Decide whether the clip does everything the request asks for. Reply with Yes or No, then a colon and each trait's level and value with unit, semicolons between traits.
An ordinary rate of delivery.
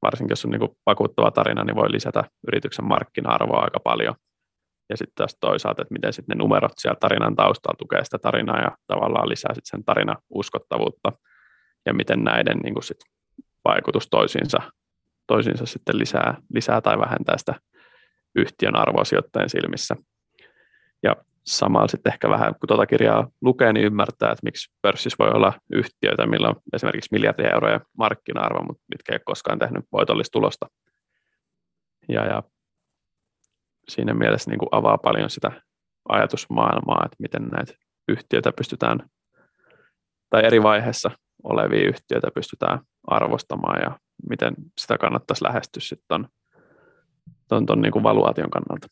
Yes: average, 140 wpm